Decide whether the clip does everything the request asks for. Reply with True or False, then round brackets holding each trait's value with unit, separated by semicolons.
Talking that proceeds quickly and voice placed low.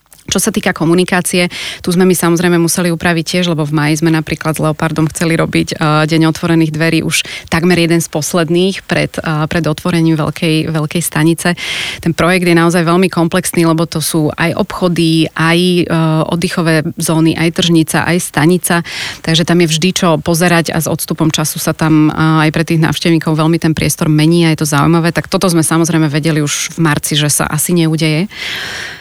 False (180 wpm; 165 Hz)